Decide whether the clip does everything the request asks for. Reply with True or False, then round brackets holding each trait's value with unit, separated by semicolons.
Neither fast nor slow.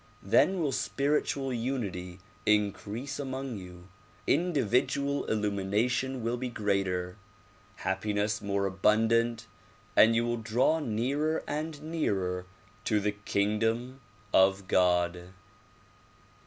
False (100 wpm)